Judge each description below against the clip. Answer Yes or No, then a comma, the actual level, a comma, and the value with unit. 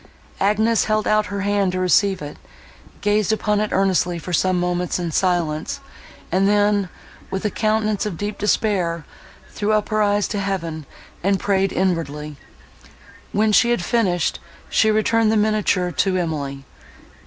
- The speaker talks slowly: No, average, 155 wpm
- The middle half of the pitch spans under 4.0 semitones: Yes, average, 3.1 semitones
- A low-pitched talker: No, high, 195 Hz